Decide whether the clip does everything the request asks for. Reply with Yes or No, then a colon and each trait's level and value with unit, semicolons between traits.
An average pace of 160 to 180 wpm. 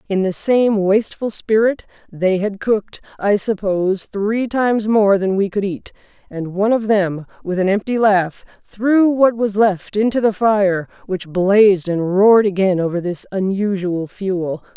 Yes: average, 165 wpm